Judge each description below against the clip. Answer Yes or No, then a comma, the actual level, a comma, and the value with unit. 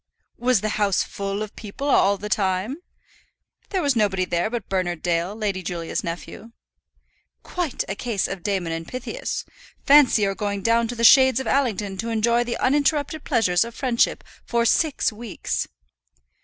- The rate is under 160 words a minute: No, average, 165 wpm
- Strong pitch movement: No, average, 4.3 semitones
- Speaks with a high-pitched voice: Yes, high, 215 Hz